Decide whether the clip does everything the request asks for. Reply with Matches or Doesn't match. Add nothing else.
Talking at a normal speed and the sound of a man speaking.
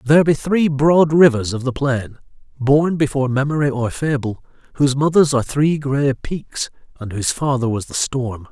Matches